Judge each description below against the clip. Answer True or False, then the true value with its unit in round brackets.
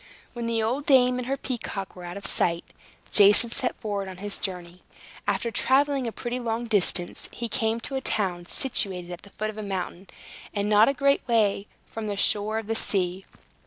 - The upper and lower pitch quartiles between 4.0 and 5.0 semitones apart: False (3.6 semitones)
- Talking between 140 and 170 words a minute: False (200 wpm)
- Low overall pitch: False (215 Hz)